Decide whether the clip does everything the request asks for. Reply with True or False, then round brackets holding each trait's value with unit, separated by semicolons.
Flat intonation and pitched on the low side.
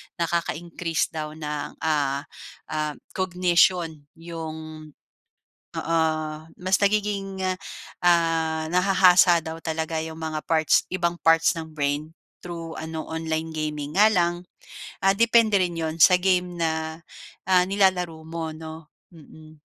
False (2.1 semitones; 165 Hz)